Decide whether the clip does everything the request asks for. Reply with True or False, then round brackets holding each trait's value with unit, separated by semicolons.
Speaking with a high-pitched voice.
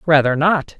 False (155 Hz)